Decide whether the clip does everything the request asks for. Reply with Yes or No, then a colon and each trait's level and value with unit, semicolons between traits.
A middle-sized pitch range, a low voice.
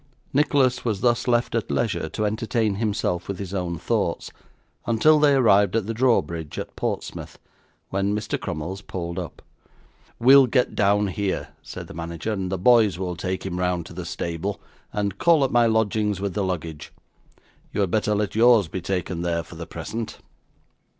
Yes: average, 4.1 semitones; low, 100 Hz